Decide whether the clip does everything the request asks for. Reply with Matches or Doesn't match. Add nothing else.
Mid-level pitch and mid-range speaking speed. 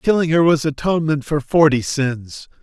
Matches